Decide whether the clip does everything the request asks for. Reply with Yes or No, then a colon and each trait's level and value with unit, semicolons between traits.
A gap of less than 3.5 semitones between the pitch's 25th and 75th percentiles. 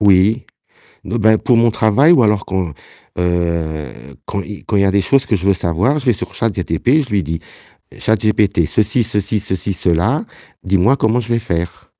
No: average, 4.1 semitones